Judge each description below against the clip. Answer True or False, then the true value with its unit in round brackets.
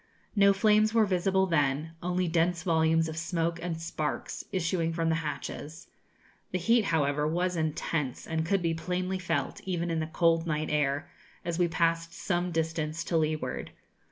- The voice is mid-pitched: True (165 Hz)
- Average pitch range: False (2.0 semitones)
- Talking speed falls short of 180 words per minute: True (165 wpm)